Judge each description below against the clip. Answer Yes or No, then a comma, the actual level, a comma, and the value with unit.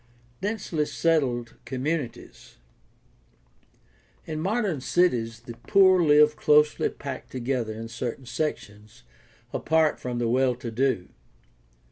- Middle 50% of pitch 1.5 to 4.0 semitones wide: No, average, 4.9 semitones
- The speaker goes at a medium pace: No, slow, 110 wpm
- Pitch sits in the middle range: No, low, 130 Hz